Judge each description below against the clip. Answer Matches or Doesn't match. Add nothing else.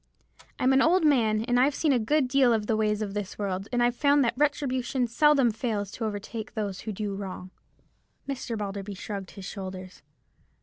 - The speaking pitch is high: Matches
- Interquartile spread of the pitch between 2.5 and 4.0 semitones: Doesn't match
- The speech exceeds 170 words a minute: Matches